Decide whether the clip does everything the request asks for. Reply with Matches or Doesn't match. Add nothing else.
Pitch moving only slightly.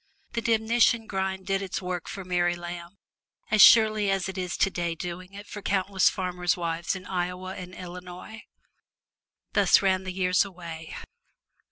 Matches